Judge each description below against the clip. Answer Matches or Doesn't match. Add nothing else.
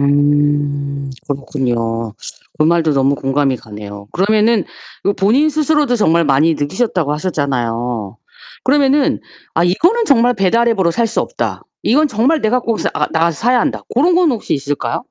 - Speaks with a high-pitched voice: Doesn't match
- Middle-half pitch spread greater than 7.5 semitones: Matches